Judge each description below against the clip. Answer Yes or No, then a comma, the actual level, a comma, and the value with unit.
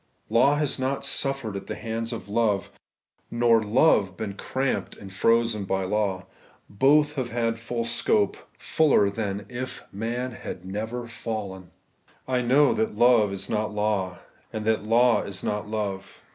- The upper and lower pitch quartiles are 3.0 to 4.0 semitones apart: Yes, average, 3.3 semitones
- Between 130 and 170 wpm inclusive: Yes, average, 160 wpm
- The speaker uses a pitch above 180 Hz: No, low, 110 Hz